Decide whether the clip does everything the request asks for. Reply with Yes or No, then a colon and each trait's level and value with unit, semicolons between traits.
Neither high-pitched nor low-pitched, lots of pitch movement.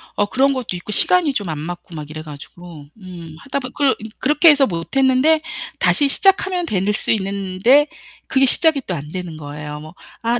No: high, 205 Hz; wide, 8.7 semitones